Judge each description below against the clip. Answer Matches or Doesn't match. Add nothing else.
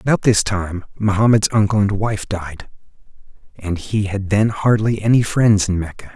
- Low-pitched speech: Matches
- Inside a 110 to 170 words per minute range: Matches